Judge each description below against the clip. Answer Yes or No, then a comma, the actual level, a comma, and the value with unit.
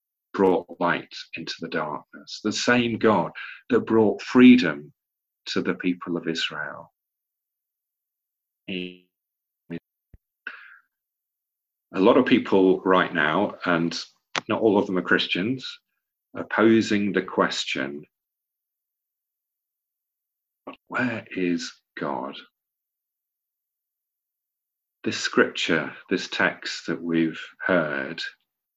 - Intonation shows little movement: No, average, 4.2 semitones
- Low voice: Yes, very low, 90 Hz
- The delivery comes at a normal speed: No, slow, 90 wpm